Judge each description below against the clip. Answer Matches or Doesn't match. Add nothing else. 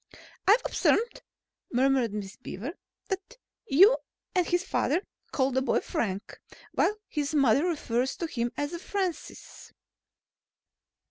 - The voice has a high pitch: Matches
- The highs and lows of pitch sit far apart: Matches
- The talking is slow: Matches